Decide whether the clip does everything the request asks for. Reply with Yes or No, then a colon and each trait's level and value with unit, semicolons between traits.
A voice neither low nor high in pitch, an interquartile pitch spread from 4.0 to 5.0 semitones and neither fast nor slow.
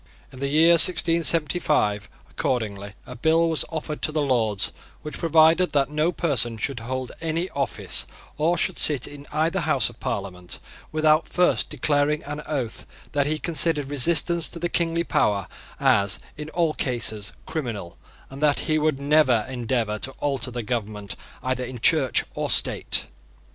Yes: medium, 145 Hz; average, 4.7 semitones; average, 160 wpm